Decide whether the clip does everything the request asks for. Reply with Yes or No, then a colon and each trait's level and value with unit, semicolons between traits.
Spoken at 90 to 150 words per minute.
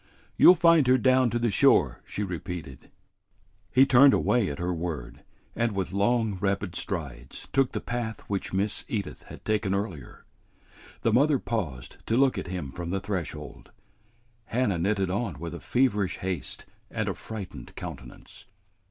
No: average, 160 wpm